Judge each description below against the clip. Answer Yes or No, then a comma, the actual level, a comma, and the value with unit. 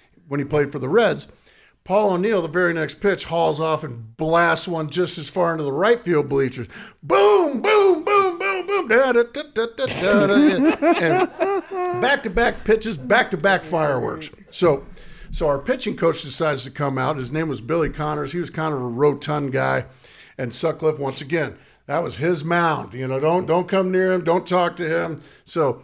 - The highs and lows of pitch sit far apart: Yes, wide, 6.7 semitones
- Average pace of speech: Yes, average, 185 wpm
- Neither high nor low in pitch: Yes, medium, 170 Hz